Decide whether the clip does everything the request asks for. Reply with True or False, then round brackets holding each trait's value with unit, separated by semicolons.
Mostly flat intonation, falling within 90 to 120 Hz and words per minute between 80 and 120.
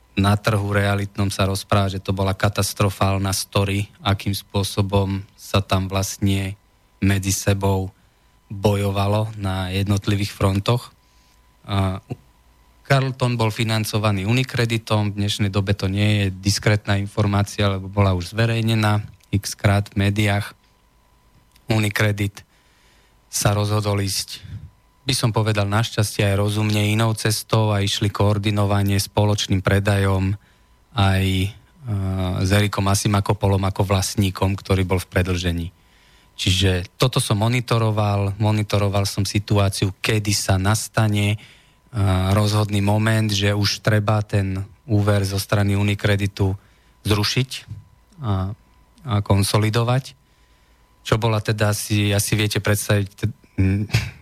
True (1.6 semitones; 100 Hz; 110 wpm)